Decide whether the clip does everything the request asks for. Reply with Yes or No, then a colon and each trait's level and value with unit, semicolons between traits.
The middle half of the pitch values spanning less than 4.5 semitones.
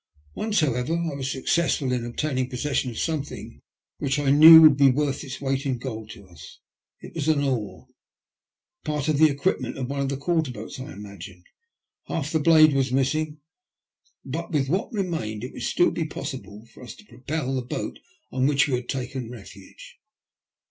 Yes: average, 3.6 semitones